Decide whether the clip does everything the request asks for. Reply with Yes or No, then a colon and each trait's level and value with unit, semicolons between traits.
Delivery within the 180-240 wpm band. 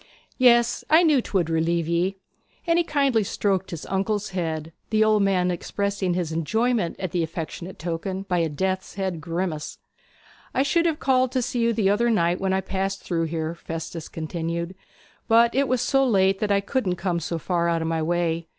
Yes: average, 195 wpm